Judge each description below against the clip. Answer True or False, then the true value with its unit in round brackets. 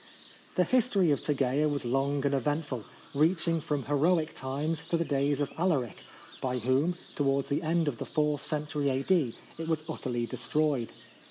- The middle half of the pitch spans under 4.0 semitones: True (2.9 semitones)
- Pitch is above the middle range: False (145 Hz)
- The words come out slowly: False (165 wpm)